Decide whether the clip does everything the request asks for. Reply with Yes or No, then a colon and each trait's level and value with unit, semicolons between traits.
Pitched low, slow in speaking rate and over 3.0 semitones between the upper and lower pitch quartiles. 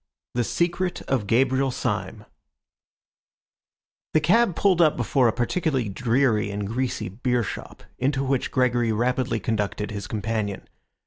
Yes: low, 125 Hz; slow, 125 wpm; average, 4.0 semitones